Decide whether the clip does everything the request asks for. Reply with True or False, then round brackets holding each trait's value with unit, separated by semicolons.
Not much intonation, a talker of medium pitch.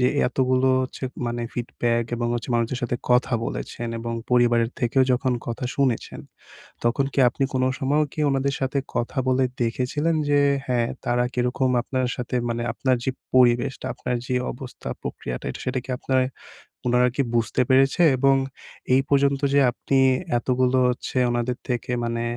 False (1.7 semitones; 125 Hz)